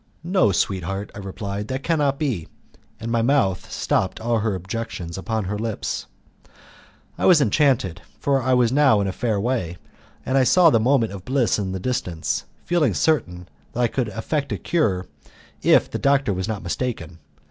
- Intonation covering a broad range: Yes, wide, 5.7 semitones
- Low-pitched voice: Yes, low, 115 Hz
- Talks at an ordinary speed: Yes, average, 180 wpm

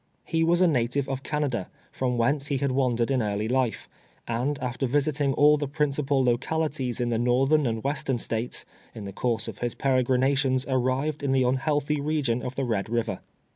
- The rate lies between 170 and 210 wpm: Yes, average, 195 wpm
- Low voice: Yes, low, 130 Hz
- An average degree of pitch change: Yes, average, 3.0 semitones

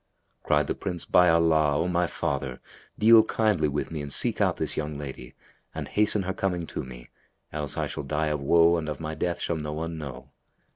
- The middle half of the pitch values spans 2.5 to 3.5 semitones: Yes, average, 2.8 semitones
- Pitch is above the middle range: No, very low, 80 Hz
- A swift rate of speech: Yes, fast, 210 wpm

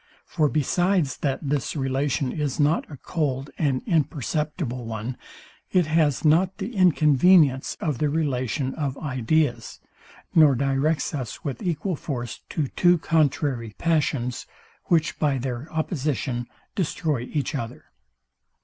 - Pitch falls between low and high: Yes, medium, 145 Hz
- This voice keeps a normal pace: No, slow, 125 wpm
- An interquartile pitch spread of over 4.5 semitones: No, average, 3.5 semitones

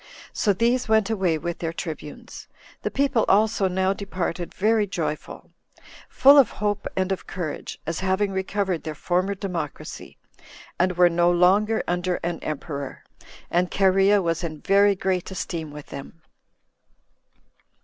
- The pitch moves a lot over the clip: No, average, 3.0 semitones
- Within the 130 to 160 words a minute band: Yes, average, 140 wpm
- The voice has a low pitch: No, medium, 185 Hz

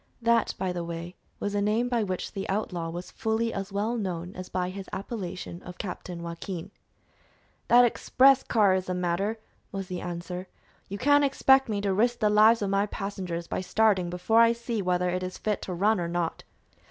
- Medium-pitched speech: No, high, 195 Hz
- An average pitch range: Yes, average, 3.7 semitones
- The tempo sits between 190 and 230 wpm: Yes, average, 200 wpm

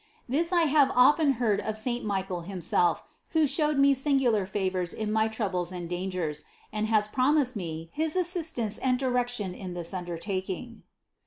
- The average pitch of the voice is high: Yes, high, 220 Hz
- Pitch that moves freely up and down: Yes, wide, 6.5 semitones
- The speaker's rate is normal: Yes, average, 165 wpm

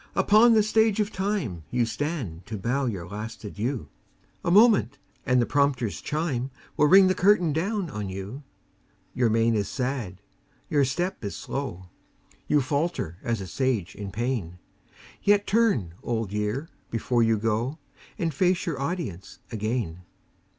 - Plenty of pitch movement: Yes, wide, 8.1 semitones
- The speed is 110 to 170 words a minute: Yes, average, 150 wpm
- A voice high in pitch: No, low, 125 Hz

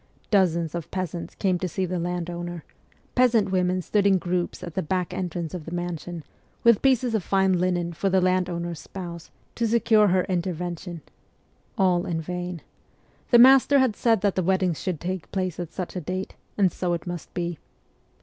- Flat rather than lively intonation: Yes, narrow, 1.8 semitones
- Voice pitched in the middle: Yes, medium, 180 Hz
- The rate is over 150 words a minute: Yes, average, 180 wpm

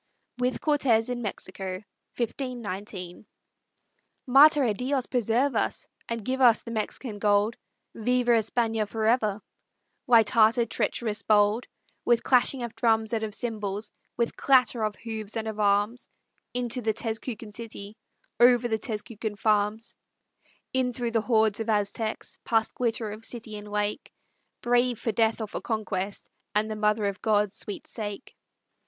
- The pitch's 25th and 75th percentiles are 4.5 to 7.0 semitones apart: No, narrow, 2.4 semitones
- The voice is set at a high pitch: Yes, high, 225 Hz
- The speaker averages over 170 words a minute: No, average, 145 wpm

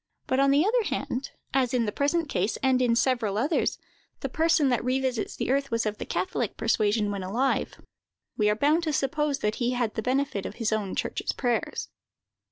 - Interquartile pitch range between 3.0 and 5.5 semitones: Yes, average, 4.2 semitones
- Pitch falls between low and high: No, very high, 250 Hz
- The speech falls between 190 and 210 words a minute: Yes, average, 200 wpm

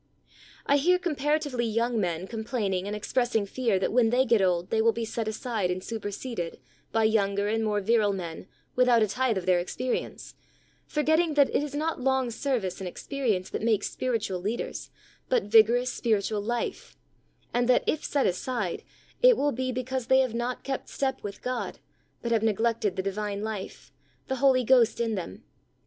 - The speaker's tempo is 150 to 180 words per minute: No, average, 190 wpm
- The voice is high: Yes, high, 230 Hz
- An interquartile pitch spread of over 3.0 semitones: Yes, average, 3.9 semitones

